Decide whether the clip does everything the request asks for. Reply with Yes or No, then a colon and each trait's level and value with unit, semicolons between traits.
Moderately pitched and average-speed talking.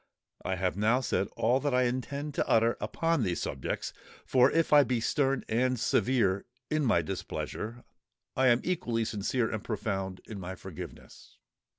No: low, 120 Hz; average, 165 wpm